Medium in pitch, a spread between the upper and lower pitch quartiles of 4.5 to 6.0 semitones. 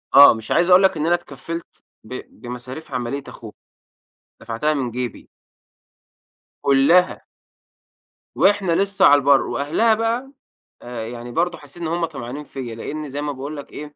Yes: medium, 145 Hz; average, 5.2 semitones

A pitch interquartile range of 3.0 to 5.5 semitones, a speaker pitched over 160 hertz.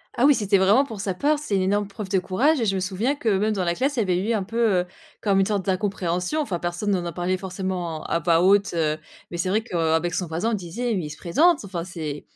Yes: average, 3.7 semitones; high, 190 Hz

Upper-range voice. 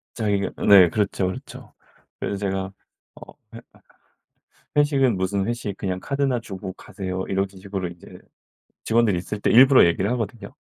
No: low, 100 Hz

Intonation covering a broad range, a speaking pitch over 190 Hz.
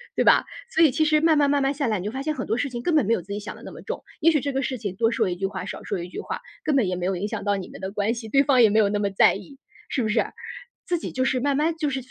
Yes: wide, 5.9 semitones; high, 240 Hz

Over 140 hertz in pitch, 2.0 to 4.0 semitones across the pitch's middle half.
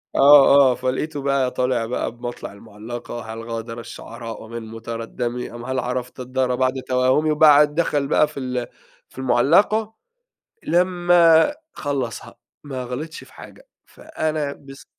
No: low, 130 Hz; average, 3.7 semitones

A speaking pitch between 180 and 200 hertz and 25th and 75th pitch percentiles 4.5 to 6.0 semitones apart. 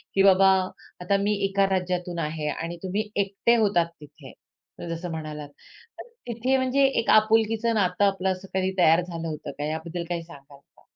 No: medium, 185 Hz; average, 3.8 semitones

